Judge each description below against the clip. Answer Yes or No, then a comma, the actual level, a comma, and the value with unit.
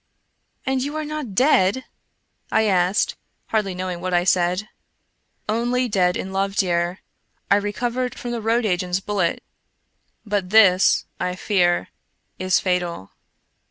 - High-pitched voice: Yes, high, 195 Hz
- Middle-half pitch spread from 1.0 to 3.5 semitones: No, average, 4.0 semitones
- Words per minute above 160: No, average, 145 wpm